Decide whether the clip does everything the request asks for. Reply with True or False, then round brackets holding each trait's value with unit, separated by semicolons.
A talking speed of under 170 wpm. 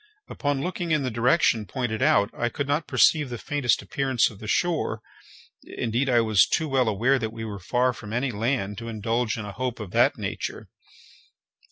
False (190 wpm)